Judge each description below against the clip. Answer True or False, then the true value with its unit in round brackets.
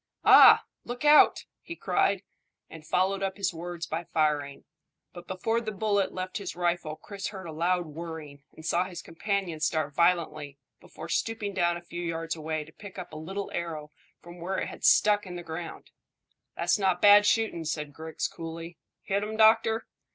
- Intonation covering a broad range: False (3.6 semitones)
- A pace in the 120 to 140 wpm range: False (180 wpm)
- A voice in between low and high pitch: True (175 Hz)